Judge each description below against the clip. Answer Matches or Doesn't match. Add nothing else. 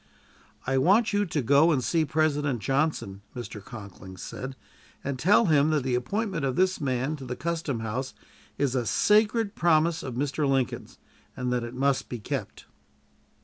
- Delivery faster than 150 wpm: Matches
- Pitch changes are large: Doesn't match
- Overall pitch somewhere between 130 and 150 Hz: Matches